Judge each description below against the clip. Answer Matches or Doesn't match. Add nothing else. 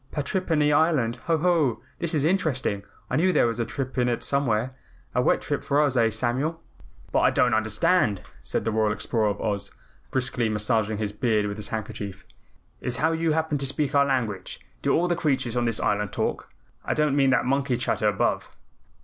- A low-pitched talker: Matches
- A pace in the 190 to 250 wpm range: Matches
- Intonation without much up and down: Doesn't match